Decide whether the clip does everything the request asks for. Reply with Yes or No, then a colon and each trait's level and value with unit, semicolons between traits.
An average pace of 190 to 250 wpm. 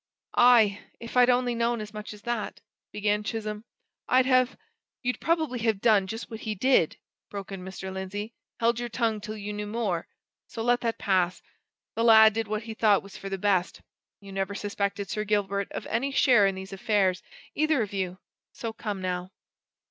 Yes: average, 195 wpm